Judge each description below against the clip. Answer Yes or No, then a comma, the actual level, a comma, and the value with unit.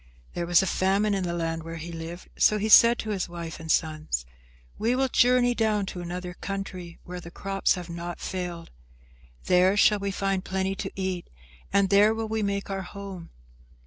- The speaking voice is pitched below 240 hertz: Yes, high, 190 Hz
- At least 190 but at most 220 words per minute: Yes, average, 195 wpm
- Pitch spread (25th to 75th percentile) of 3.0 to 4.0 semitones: No, narrow, 2.6 semitones